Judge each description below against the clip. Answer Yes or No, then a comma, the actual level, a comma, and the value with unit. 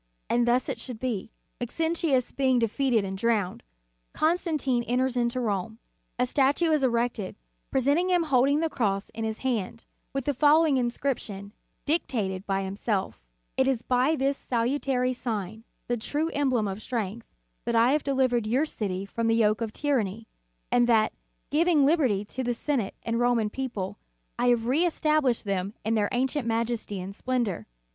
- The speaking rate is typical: Yes, average, 165 wpm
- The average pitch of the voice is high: Yes, high, 245 Hz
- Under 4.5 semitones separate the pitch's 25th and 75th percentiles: Yes, average, 3.8 semitones